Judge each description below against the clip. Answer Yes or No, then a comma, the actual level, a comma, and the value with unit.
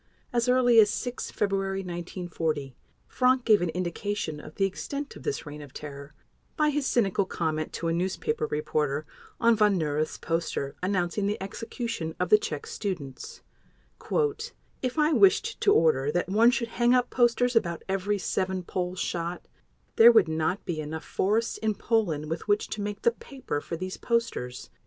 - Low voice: No, high, 195 Hz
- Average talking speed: Yes, average, 170 wpm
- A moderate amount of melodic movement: No, wide, 6.4 semitones